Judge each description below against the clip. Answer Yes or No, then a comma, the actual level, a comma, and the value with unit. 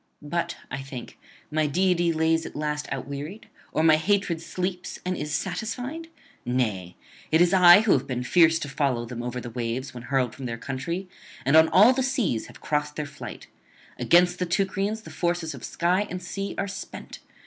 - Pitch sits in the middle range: Yes, medium, 160 Hz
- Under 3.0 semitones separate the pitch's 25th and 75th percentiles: No, average, 5.3 semitones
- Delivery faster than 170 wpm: Yes, average, 190 wpm